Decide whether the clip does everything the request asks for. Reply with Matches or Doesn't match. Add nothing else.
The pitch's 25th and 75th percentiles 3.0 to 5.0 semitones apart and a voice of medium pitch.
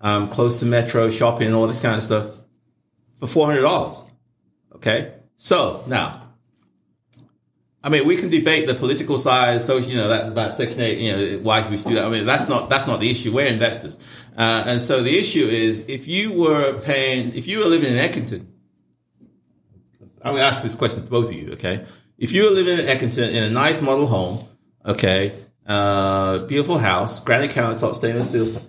Doesn't match